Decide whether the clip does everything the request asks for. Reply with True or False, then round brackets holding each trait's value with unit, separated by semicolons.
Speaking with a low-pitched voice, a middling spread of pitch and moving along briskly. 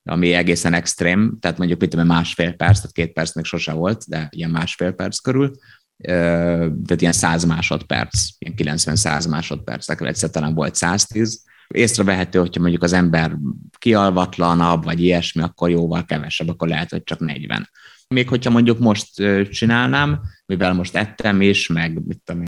True (85 Hz; 3.2 semitones; 160 wpm)